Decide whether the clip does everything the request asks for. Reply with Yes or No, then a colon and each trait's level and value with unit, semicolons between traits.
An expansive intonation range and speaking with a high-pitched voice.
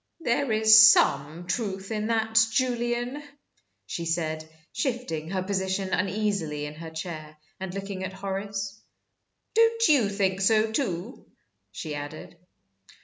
No: average, 4.7 semitones; high, 195 Hz